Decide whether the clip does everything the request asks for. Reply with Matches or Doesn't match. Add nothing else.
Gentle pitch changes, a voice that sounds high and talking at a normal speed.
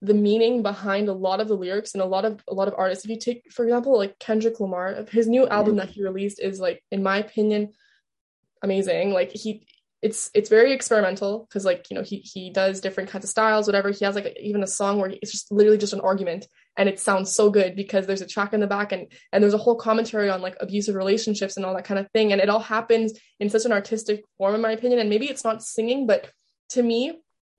Doesn't match